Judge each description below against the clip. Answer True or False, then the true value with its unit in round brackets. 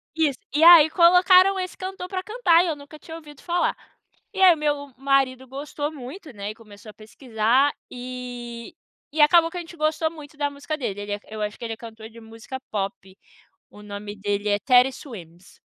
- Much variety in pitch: True (6.5 semitones)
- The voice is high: True (275 Hz)